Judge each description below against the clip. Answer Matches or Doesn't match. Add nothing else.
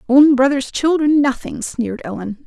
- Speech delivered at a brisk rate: Doesn't match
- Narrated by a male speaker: Doesn't match